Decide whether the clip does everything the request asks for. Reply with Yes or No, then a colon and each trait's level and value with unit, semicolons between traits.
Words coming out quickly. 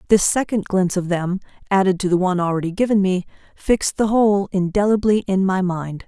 No: average, 190 wpm